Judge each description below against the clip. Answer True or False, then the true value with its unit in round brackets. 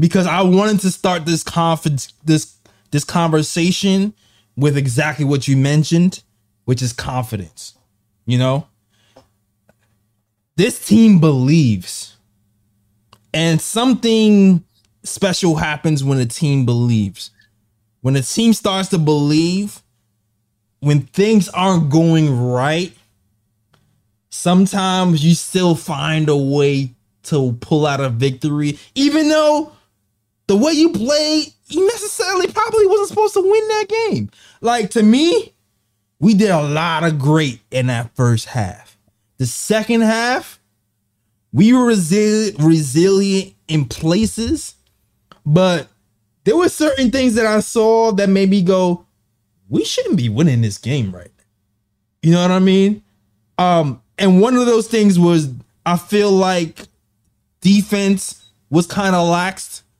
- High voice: False (155 Hz)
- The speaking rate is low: True (130 wpm)